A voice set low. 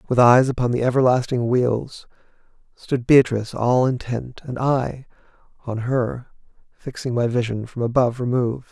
Yes: low, 125 Hz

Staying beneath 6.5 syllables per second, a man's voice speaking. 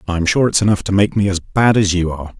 Yes: 6.3 syllables/s; male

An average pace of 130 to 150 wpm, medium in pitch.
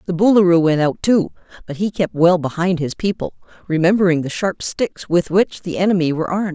No: average, 200 wpm; medium, 180 Hz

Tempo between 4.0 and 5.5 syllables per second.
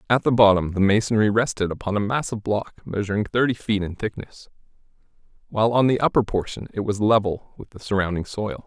No: 6.0 syllables/s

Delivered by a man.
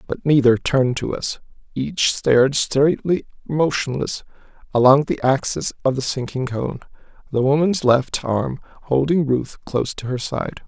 Yes: male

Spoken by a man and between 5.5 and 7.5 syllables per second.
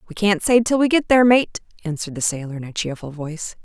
No: female; 6.6 syllables/s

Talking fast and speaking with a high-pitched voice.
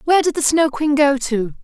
Yes: fast, 260 wpm; very high, 285 Hz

